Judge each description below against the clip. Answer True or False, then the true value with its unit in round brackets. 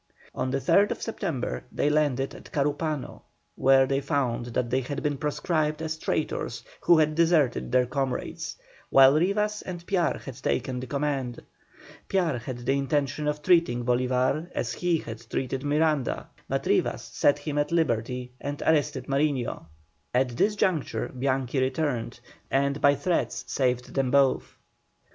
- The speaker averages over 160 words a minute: False (150 wpm)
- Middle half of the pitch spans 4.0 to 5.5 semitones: False (3.1 semitones)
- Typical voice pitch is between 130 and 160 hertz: True (140 Hz)